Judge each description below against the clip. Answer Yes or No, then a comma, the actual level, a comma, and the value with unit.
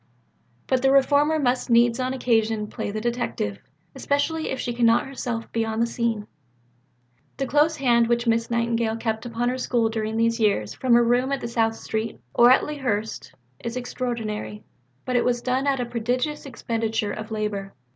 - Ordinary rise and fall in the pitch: No, narrow, 2.3 semitones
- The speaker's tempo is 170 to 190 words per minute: Yes, average, 180 wpm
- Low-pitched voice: No, high, 235 Hz